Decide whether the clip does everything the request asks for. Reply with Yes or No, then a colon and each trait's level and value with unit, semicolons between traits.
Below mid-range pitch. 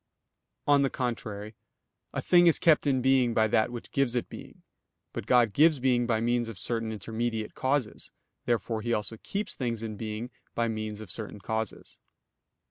Yes: low, 115 Hz